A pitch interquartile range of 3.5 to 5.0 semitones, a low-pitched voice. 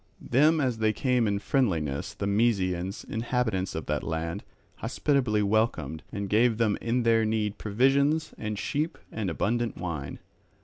Yes: average, 3.9 semitones; low, 110 Hz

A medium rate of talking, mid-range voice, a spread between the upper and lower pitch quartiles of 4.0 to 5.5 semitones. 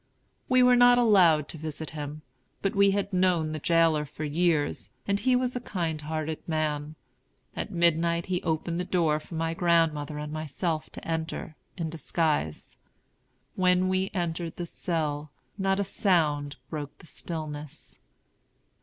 No: average, 155 wpm; medium, 165 Hz; average, 3.0 semitones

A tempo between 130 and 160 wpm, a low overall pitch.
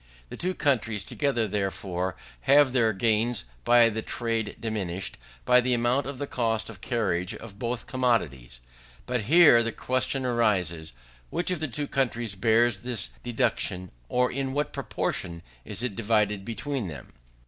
Yes: average, 155 wpm; low, 115 Hz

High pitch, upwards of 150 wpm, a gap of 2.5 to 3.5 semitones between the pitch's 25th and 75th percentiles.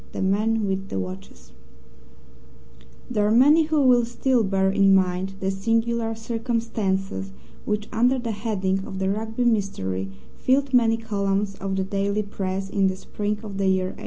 Yes: high, 205 Hz; average, 165 wpm; average, 2.9 semitones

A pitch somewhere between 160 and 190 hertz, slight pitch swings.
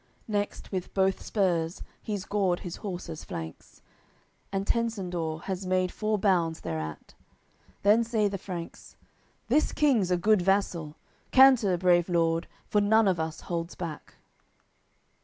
No: medium, 185 Hz; average, 3.5 semitones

